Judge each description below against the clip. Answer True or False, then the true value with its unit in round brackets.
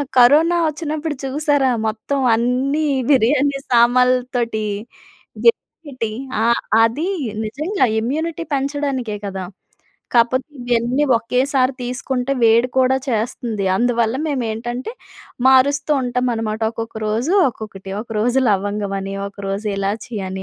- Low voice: False (245 Hz)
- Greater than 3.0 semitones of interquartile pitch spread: True (3.7 semitones)